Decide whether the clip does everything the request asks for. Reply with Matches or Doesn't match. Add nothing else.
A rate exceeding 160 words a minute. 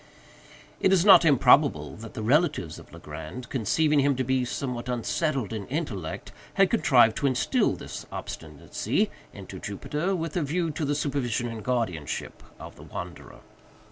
Doesn't match